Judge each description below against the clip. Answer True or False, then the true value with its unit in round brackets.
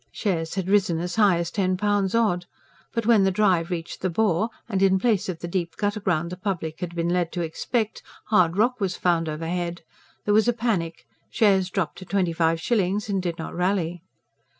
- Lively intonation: False (3.2 semitones)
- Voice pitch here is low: False (185 Hz)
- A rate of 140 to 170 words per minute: False (205 wpm)